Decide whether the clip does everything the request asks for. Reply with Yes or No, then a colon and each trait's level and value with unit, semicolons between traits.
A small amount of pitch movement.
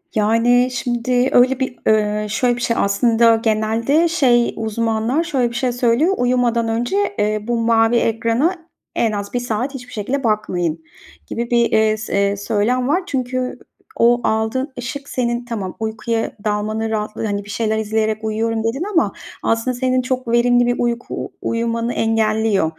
Yes: narrow, 2.2 semitones